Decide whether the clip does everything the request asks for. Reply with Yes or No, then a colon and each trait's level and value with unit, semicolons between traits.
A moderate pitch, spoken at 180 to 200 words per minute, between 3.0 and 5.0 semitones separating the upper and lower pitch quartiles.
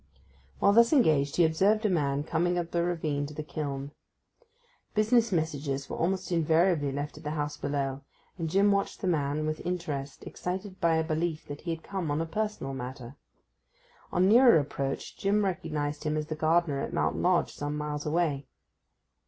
Yes: medium, 160 Hz; average, 185 wpm; average, 3.6 semitones